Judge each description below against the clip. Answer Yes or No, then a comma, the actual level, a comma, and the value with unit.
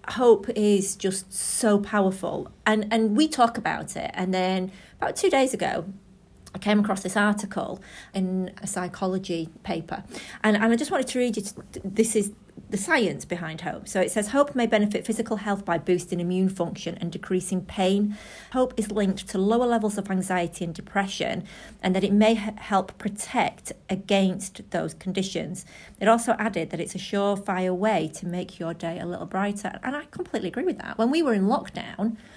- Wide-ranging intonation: No, average, 3.1 semitones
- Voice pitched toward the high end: Yes, high, 200 Hz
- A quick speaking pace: No, average, 190 wpm